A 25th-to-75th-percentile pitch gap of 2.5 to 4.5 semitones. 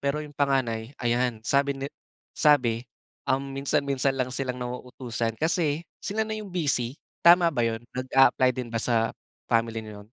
Yes: average, 3.4 semitones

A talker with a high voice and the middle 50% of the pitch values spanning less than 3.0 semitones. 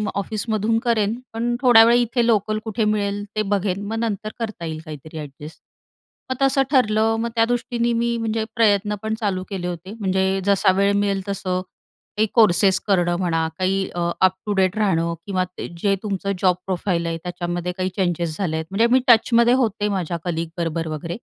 No: high, 200 Hz; average, 3.7 semitones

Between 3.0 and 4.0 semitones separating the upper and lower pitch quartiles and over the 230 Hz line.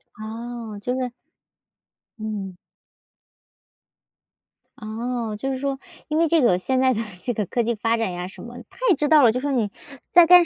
Yes: average, 3.5 semitones; high, 240 Hz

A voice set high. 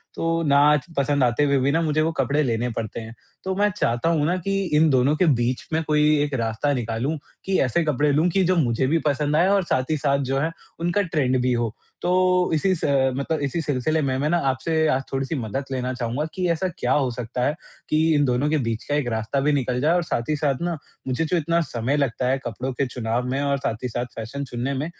No: medium, 140 Hz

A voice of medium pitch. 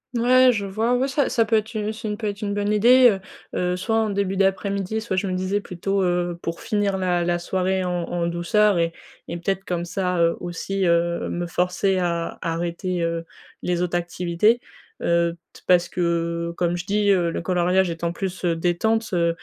Yes: medium, 180 Hz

